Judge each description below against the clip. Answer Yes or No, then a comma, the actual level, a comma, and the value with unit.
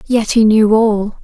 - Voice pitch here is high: Yes, high, 215 Hz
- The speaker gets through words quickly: No, average, 195 wpm